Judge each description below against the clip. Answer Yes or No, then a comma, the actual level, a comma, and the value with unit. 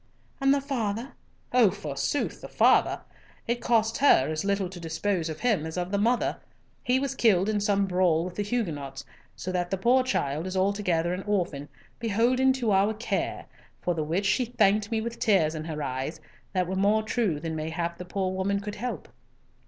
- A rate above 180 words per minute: Yes, average, 190 wpm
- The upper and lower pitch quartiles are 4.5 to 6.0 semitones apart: Yes, average, 4.9 semitones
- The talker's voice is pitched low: No, high, 195 Hz